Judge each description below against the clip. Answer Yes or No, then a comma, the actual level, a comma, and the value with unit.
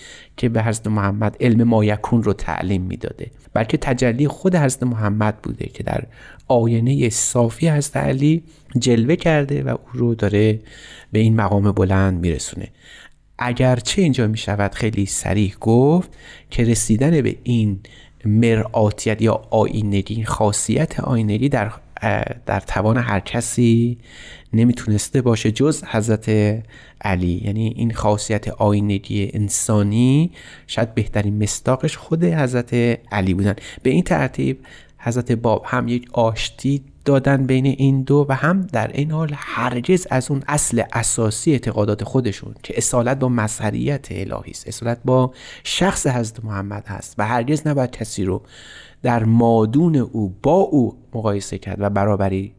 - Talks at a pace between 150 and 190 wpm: No, average, 135 wpm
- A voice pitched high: No, low, 115 Hz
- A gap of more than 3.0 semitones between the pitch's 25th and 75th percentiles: Yes, average, 3.8 semitones